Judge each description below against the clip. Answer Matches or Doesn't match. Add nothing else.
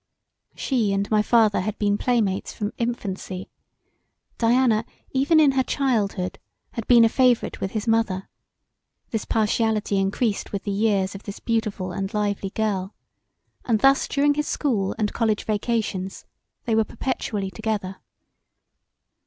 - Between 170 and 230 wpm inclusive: Doesn't match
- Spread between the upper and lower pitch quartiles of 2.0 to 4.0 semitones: Matches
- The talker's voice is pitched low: Doesn't match